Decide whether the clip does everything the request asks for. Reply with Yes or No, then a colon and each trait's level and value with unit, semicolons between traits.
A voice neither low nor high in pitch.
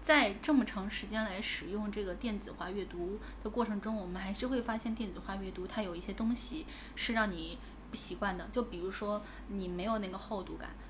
No: high, 210 Hz